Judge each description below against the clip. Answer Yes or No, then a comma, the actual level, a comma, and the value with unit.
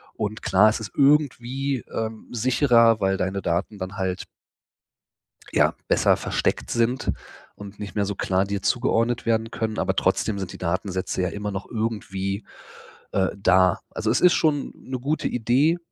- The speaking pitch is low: Yes, low, 110 Hz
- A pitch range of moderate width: Yes, average, 3.8 semitones